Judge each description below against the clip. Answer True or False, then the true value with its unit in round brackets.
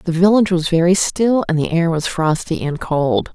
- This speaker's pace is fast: True (215 wpm)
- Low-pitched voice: False (175 Hz)